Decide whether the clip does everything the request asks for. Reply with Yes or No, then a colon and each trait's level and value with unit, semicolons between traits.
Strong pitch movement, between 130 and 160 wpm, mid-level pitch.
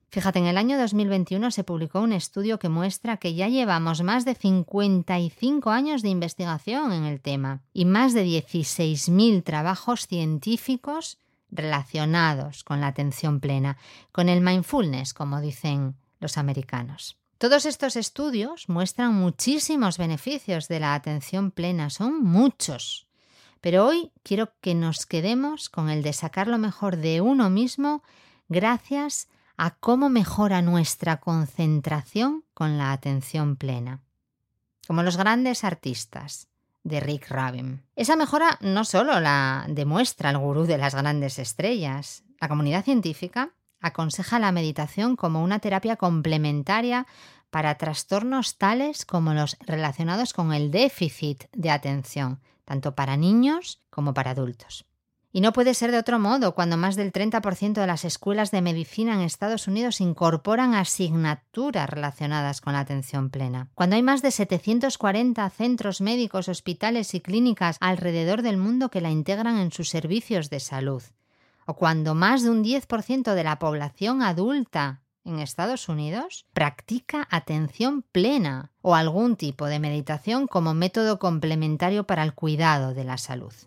Yes: wide, 6.8 semitones; average, 145 wpm; medium, 180 Hz